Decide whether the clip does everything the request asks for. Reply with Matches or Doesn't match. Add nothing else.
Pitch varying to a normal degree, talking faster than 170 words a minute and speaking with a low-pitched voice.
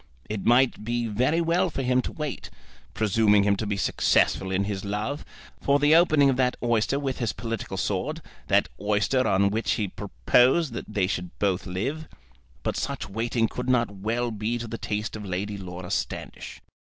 Matches